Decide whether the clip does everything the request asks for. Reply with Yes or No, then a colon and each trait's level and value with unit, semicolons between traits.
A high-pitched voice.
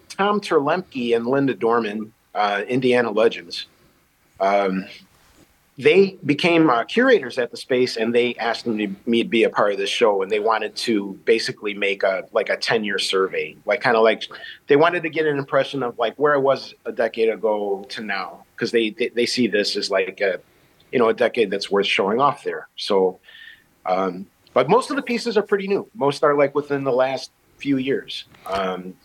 No: low, 135 Hz